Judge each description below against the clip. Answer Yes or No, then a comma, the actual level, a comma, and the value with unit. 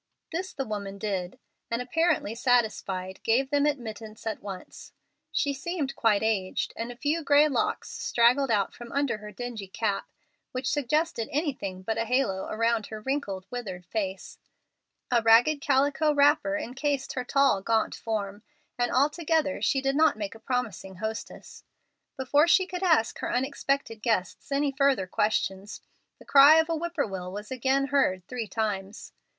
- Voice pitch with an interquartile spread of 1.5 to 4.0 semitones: No, average, 5.2 semitones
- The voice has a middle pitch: No, high, 245 Hz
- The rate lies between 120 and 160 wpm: Yes, average, 155 wpm